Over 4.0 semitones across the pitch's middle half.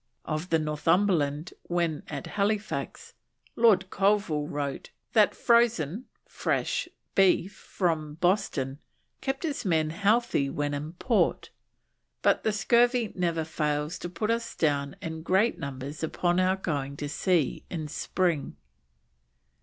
Yes: wide, 5.4 semitones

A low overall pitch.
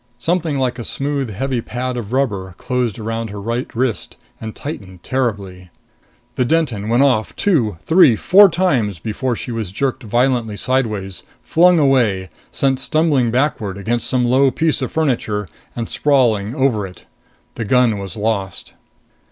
Yes: low, 120 Hz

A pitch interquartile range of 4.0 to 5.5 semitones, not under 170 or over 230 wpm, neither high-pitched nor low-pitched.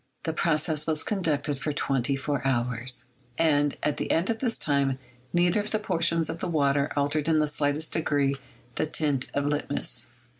No: average, 2.7 semitones; average, 180 wpm; medium, 150 Hz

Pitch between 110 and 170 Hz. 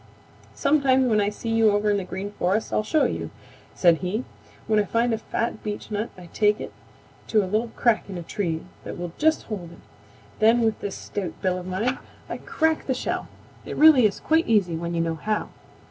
No: high, 210 Hz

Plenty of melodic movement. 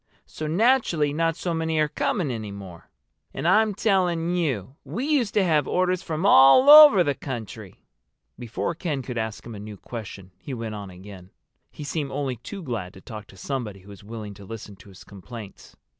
Yes: wide, 8.5 semitones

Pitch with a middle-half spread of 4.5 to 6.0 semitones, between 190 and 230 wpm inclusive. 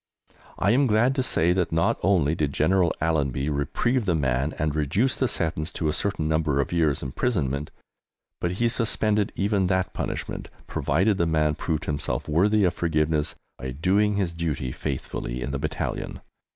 No: average, 5.0 semitones; average, 170 wpm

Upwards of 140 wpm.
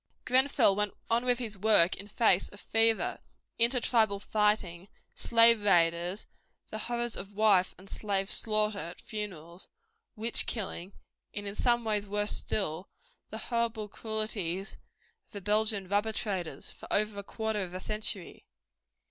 Yes: average, 150 wpm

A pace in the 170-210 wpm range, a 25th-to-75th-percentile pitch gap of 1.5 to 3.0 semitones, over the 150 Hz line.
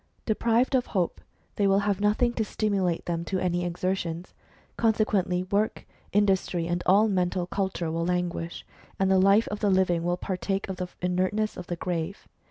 Yes: average, 180 wpm; narrow, 2.6 semitones; high, 190 Hz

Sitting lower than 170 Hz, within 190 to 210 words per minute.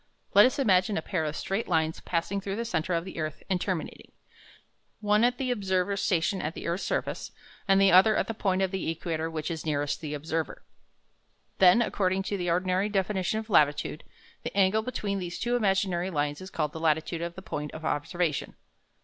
No: medium, 185 Hz; average, 200 wpm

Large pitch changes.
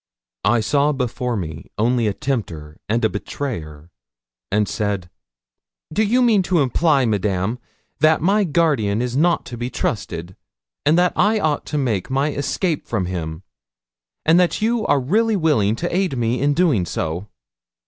Yes: wide, 8.0 semitones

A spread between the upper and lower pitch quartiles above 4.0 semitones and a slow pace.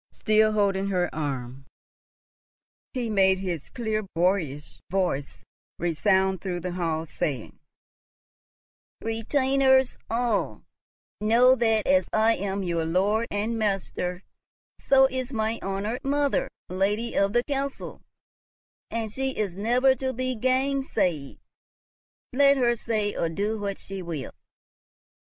Yes: average, 5.0 semitones; slow, 120 wpm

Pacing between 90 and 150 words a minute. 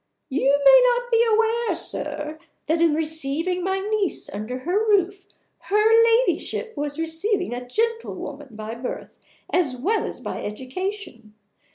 Yes: average, 140 wpm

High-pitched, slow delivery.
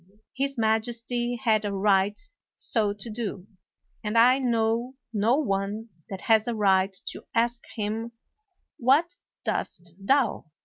Yes: high, 225 Hz; slow, 130 wpm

